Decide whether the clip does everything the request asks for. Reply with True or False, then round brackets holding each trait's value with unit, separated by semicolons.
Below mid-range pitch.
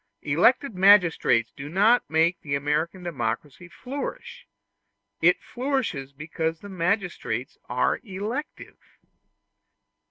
False (170 Hz)